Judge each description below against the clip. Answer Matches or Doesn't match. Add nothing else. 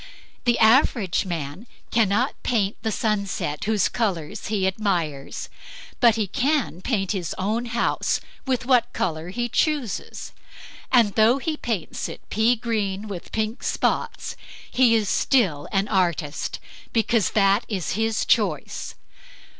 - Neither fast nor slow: Doesn't match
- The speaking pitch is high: Matches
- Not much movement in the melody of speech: Doesn't match